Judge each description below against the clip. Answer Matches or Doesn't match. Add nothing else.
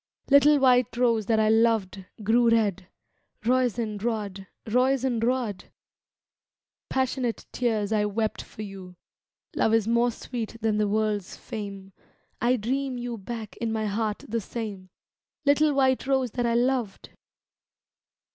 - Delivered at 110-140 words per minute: Matches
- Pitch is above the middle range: Matches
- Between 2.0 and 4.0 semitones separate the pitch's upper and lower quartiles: Matches